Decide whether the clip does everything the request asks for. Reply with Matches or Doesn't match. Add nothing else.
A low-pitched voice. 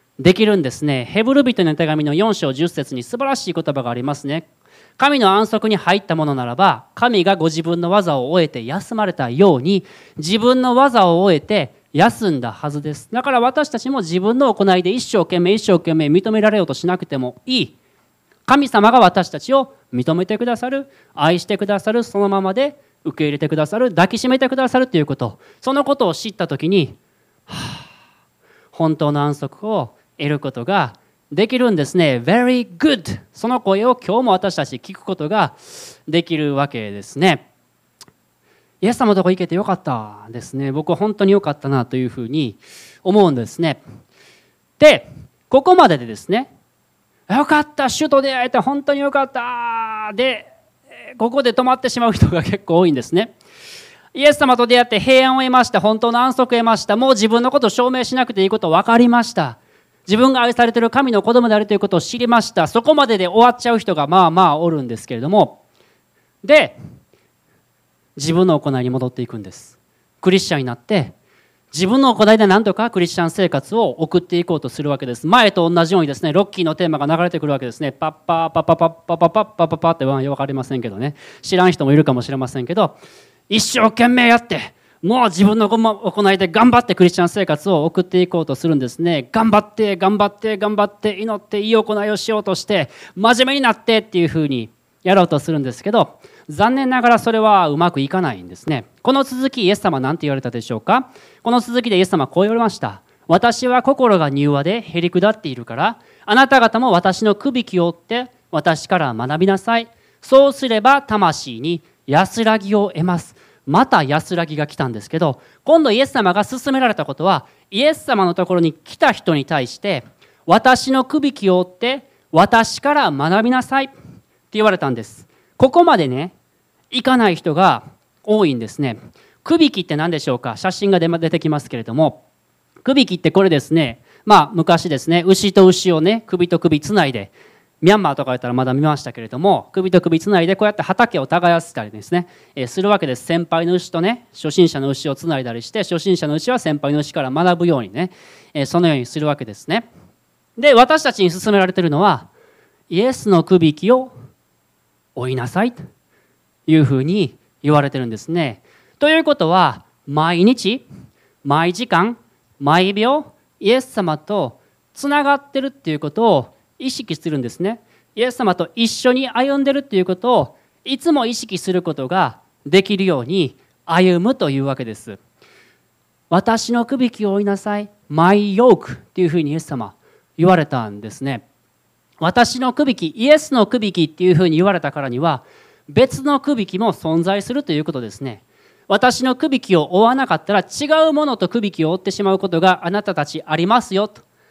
Doesn't match